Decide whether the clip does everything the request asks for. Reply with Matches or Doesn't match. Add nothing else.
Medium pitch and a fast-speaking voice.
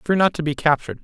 Matches